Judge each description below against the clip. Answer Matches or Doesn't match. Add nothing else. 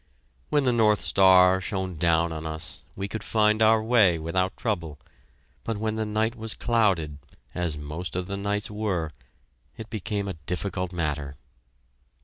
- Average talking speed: Matches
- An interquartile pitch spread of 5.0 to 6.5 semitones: Doesn't match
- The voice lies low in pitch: Matches